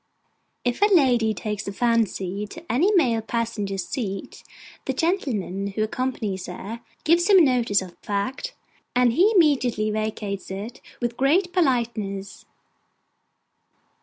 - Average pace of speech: No, slow, 130 wpm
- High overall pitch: Yes, high, 230 Hz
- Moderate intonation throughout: Yes, average, 5.0 semitones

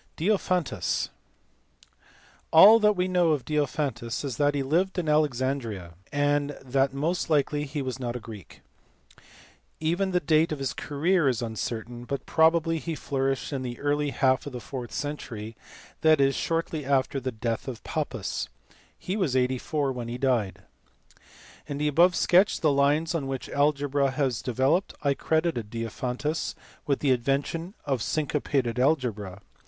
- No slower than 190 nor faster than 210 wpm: No, average, 160 wpm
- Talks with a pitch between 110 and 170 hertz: Yes, medium, 140 Hz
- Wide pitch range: No, average, 3.8 semitones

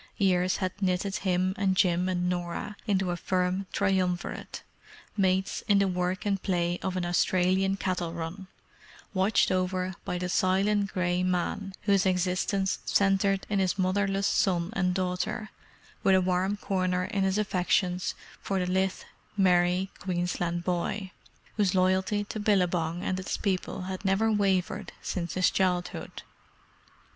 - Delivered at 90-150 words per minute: Yes, average, 140 wpm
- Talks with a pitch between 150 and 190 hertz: Yes, medium, 185 Hz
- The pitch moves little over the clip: Yes, narrow, 1.4 semitones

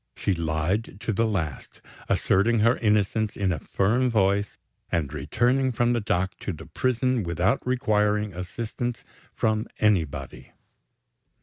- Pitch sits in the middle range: No, low, 105 Hz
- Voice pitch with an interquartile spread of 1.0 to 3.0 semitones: No, average, 4.1 semitones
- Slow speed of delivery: Yes, slow, 130 wpm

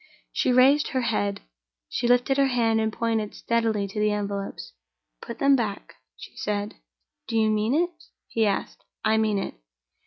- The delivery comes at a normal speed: Yes, average, 165 wpm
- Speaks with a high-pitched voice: Yes, high, 220 Hz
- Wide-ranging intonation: No, average, 2.9 semitones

